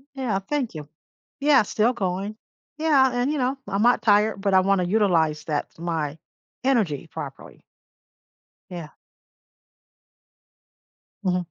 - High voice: Yes, high, 200 Hz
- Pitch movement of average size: No, wide, 5.9 semitones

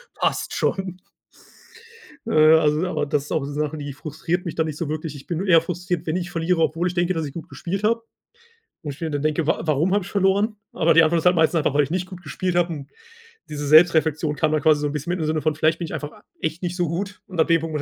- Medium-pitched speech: Yes, medium, 160 Hz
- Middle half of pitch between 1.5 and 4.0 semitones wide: Yes, average, 2.7 semitones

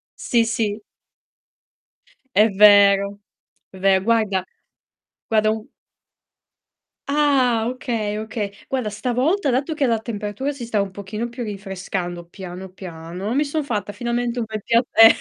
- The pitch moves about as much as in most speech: Yes, average, 3.4 semitones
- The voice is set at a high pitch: Yes, high, 215 Hz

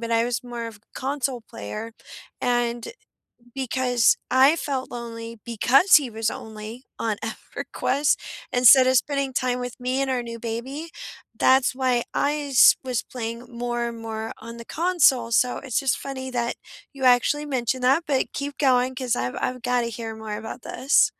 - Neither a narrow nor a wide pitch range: No, narrow, 2.2 semitones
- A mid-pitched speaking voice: No, high, 245 Hz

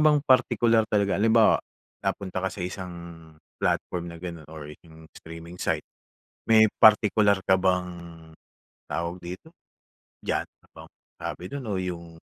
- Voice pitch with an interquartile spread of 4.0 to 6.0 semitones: Yes, average, 4.3 semitones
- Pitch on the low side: Yes, very low, 95 Hz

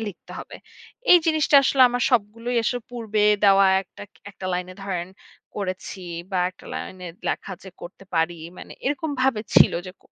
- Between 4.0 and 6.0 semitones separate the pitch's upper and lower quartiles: Yes, average, 4.9 semitones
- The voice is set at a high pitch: Yes, high, 205 Hz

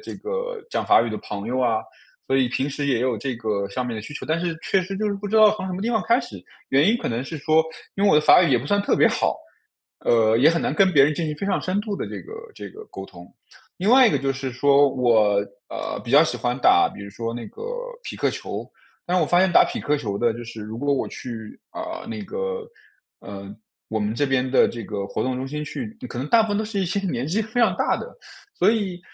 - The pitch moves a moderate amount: No, wide, 8.9 semitones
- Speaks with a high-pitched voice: No, medium, 145 Hz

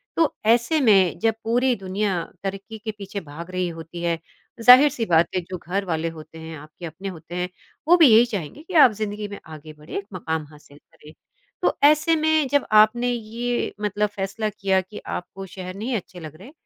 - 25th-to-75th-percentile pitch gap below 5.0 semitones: No, average, 5.3 semitones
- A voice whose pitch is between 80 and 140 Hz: No, high, 195 Hz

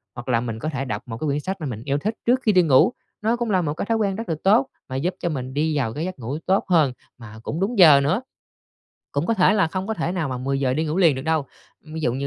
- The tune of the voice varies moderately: No, wide, 6.1 semitones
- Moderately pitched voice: Yes, medium, 155 Hz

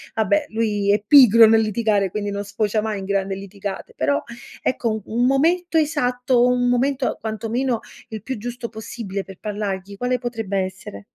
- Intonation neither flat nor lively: Yes, average, 3.6 semitones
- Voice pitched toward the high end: Yes, high, 220 Hz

